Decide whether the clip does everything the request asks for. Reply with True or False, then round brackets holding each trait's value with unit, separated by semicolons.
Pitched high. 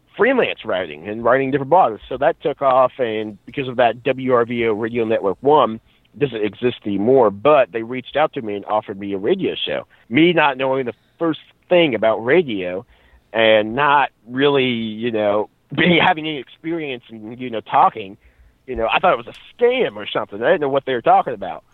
False (120 Hz)